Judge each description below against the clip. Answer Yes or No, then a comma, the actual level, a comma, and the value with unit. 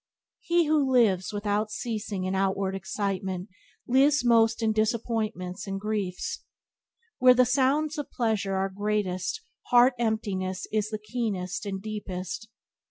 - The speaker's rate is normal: No, slow, 130 wpm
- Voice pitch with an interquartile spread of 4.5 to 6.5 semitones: No, average, 3.6 semitones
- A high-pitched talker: Yes, high, 210 Hz